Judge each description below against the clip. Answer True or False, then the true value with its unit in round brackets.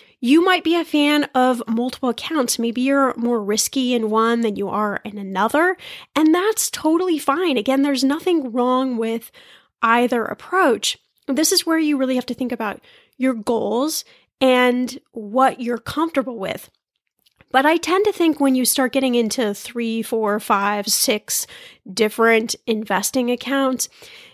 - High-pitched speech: True (255 Hz)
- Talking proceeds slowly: False (155 wpm)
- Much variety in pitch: False (4.3 semitones)